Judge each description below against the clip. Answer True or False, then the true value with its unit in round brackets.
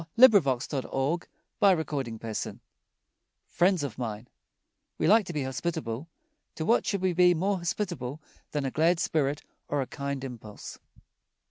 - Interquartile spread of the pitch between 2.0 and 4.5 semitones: False (5.1 semitones)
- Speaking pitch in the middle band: True (150 Hz)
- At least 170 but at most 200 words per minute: False (140 wpm)